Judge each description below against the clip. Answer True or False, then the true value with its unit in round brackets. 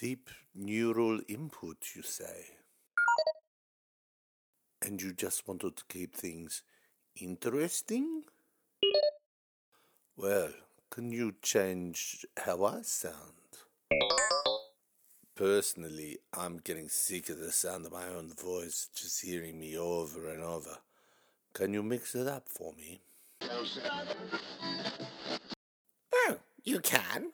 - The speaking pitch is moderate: False (95 Hz)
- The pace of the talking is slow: True (105 wpm)